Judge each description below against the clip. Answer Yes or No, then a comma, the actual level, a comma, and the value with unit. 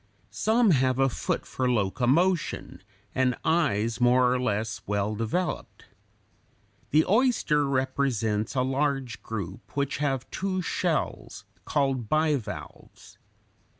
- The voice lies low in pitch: Yes, low, 130 Hz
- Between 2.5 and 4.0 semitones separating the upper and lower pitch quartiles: No, average, 4.4 semitones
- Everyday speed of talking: No, slow, 110 wpm